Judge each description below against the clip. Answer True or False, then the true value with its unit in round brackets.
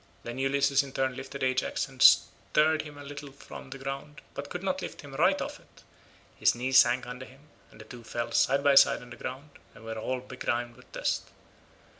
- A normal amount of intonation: False (2.2 semitones)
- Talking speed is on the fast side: True (215 wpm)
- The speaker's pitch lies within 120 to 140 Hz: True (135 Hz)